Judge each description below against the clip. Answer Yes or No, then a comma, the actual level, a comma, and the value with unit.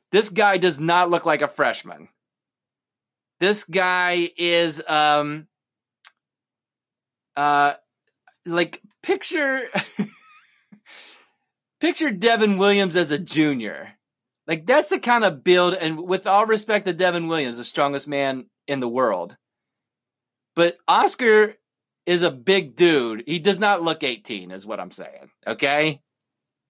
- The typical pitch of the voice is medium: Yes, medium, 170 Hz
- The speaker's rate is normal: No, slow, 125 wpm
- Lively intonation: Yes, wide, 5.9 semitones